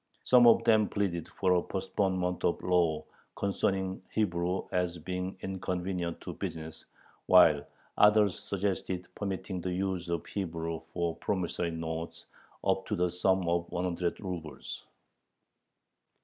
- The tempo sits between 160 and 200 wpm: No, slow, 135 wpm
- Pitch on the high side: No, very low, 90 Hz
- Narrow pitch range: Yes, narrow, 2.0 semitones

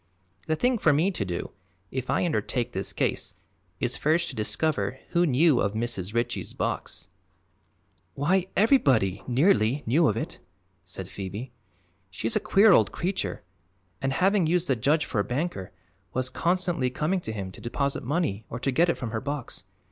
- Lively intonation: Yes, wide, 7.6 semitones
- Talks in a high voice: No, low, 130 Hz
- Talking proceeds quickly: No, average, 175 wpm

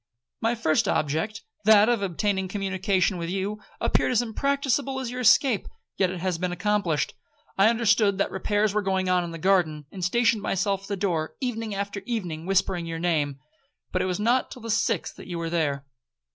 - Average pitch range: Yes, average, 3.8 semitones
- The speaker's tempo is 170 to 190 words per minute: No, average, 200 wpm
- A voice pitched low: No, high, 195 Hz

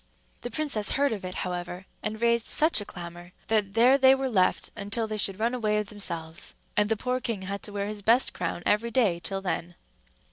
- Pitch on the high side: Yes, high, 210 Hz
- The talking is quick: Yes, fast, 215 wpm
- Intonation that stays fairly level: No, average, 3.6 semitones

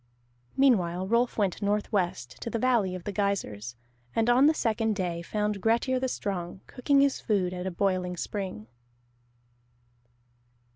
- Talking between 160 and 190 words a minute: No, average, 145 wpm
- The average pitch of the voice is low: No, high, 200 Hz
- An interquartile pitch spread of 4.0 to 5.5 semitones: Yes, average, 4.3 semitones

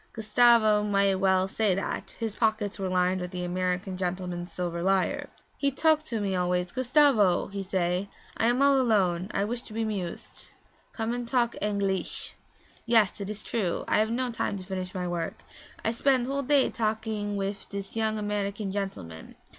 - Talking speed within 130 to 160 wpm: No, average, 180 wpm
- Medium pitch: No, high, 200 Hz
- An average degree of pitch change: Yes, average, 3.5 semitones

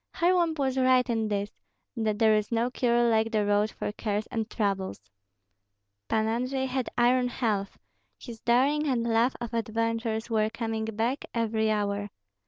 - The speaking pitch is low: No, high, 230 Hz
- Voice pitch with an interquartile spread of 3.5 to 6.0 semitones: No, narrow, 2.4 semitones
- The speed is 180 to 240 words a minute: No, average, 160 wpm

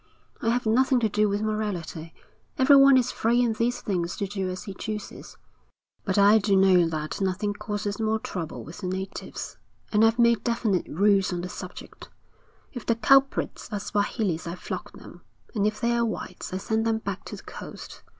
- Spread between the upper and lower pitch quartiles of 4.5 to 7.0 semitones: No, average, 3.3 semitones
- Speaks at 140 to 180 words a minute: No, average, 190 wpm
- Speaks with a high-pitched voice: Yes, high, 210 Hz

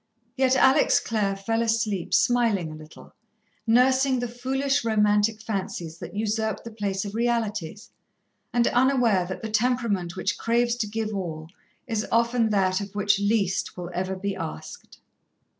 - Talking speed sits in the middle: Yes, average, 150 wpm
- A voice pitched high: Yes, high, 215 Hz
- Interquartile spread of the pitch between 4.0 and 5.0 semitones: No, average, 3.4 semitones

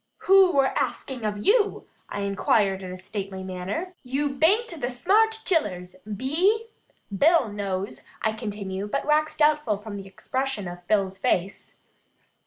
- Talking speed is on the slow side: No, average, 150 wpm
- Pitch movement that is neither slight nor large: No, wide, 7.7 semitones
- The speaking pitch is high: Yes, high, 220 Hz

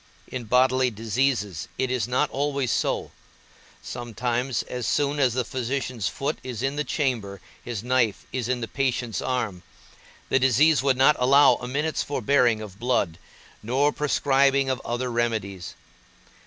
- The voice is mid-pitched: No, low, 125 Hz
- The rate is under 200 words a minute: Yes, average, 150 wpm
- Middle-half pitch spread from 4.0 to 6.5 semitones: No, average, 2.8 semitones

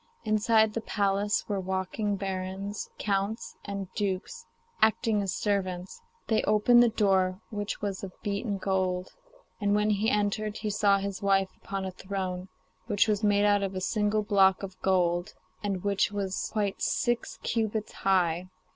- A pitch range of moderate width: No, narrow, 1.7 semitones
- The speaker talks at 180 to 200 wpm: No, average, 155 wpm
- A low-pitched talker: No, high, 200 Hz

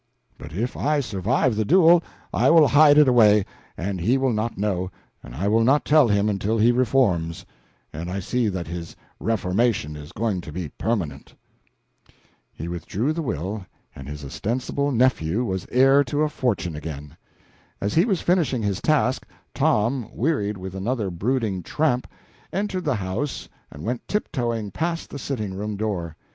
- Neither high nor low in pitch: No, low, 110 Hz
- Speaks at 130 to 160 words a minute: No, average, 170 wpm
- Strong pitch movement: Yes, wide, 6.3 semitones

